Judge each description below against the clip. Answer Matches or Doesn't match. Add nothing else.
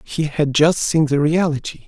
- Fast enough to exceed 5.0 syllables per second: Doesn't match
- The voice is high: Doesn't match